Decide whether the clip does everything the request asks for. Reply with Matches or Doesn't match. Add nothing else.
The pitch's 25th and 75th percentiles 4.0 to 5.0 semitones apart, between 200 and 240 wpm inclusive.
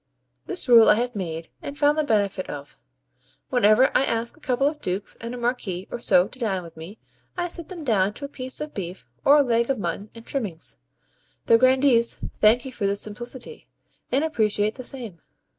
Matches